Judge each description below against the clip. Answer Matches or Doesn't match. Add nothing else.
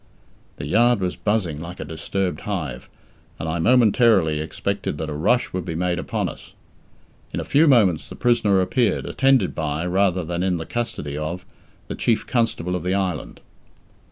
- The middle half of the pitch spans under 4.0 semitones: Doesn't match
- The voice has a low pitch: Matches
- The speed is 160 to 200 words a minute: Matches